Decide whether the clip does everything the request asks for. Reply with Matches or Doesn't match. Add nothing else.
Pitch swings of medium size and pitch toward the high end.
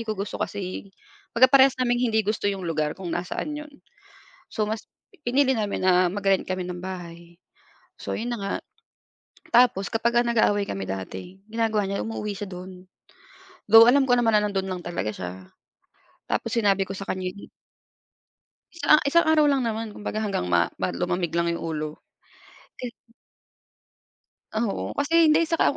Matches